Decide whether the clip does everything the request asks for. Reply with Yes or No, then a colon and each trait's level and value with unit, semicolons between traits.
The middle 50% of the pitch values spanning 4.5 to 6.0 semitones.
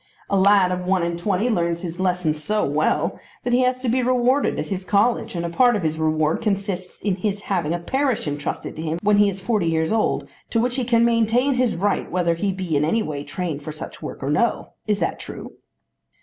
Yes: average, 5.3 semitones